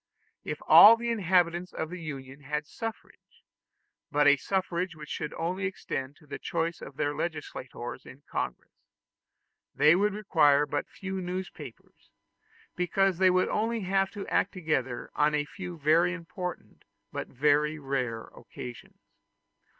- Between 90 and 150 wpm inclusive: Yes, average, 145 wpm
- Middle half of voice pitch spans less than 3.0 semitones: No, average, 4.2 semitones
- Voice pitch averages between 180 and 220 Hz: No, medium, 165 Hz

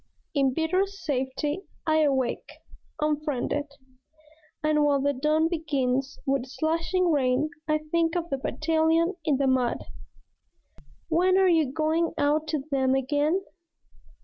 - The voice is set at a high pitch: Yes, very high, 305 Hz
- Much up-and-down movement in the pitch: No, average, 3.1 semitones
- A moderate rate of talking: No, slow, 125 wpm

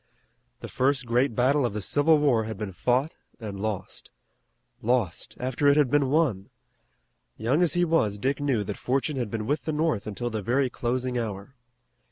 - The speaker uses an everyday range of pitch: Yes, average, 4.7 semitones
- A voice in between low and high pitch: No, low, 125 Hz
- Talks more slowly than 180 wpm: No, average, 185 wpm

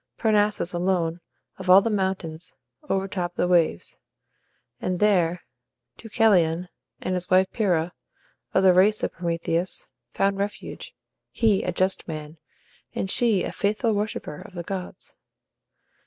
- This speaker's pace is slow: Yes, slow, 130 wpm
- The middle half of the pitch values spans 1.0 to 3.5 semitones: Yes, average, 2.7 semitones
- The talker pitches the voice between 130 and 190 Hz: Yes, medium, 185 Hz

